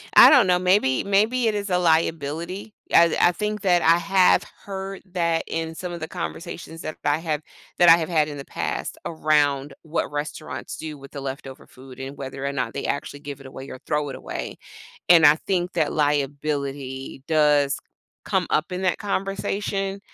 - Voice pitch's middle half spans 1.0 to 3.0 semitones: No, average, 4.2 semitones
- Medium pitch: Yes, medium, 160 Hz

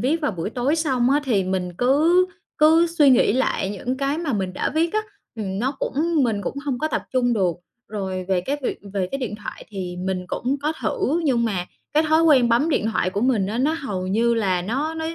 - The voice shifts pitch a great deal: Yes, wide, 7.1 semitones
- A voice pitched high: Yes, high, 245 Hz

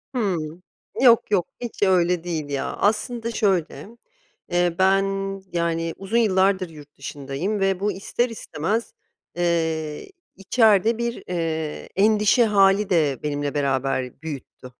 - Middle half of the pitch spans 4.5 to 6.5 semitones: Yes, average, 4.8 semitones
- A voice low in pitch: No, medium, 185 Hz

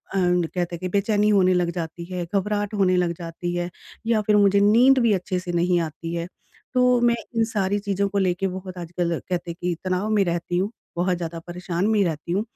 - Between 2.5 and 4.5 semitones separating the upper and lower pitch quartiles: Yes, average, 2.8 semitones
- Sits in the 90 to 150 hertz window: No, medium, 185 Hz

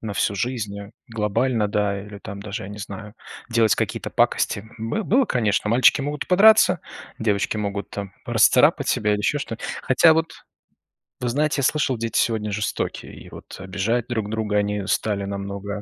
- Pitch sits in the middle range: No, low, 105 Hz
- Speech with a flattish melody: No, average, 3.3 semitones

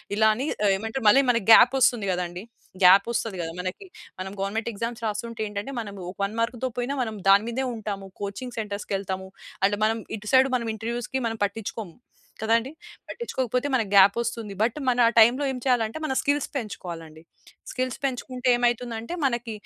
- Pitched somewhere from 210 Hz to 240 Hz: Yes, high, 225 Hz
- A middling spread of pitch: Yes, average, 3.4 semitones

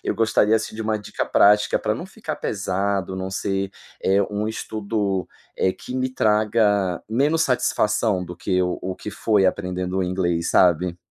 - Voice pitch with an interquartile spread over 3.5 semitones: No, average, 2.7 semitones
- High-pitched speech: No, low, 100 Hz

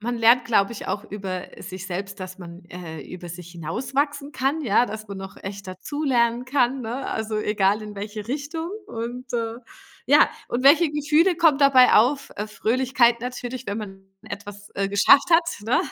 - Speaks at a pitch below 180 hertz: No, high, 230 Hz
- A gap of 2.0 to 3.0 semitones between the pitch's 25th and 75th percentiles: No, average, 5.1 semitones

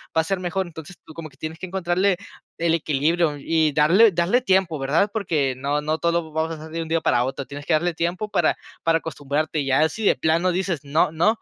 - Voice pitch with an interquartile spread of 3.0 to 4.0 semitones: No, narrow, 2.6 semitones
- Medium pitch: Yes, medium, 165 Hz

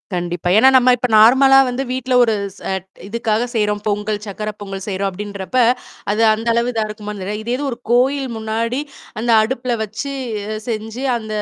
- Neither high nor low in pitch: No, high, 220 Hz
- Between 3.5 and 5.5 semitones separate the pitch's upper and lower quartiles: No, average, 2.9 semitones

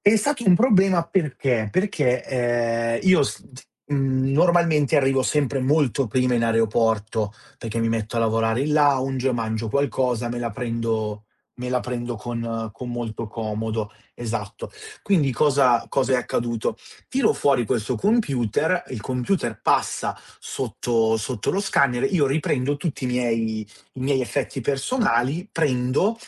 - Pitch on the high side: No, low, 125 Hz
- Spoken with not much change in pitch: No, average, 3.8 semitones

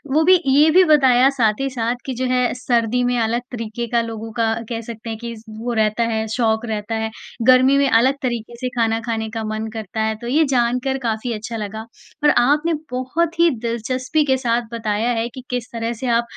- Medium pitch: No, high, 235 Hz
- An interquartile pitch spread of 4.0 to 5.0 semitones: No, narrow, 2.4 semitones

